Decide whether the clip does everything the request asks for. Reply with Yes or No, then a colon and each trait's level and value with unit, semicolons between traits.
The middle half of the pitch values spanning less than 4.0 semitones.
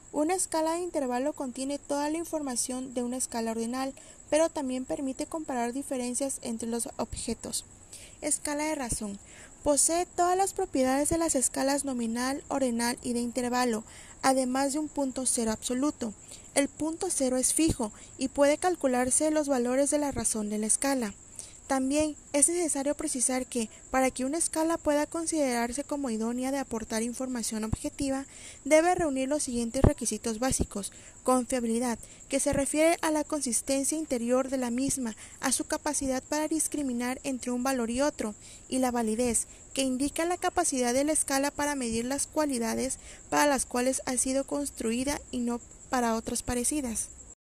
Yes: average, 3.3 semitones